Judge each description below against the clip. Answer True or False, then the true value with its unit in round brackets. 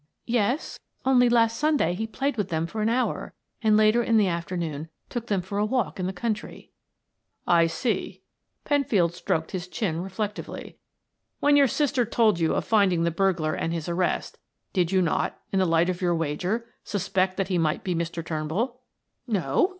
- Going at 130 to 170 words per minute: False (180 wpm)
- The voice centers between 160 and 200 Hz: True (190 Hz)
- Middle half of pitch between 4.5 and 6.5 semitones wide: True (5.2 semitones)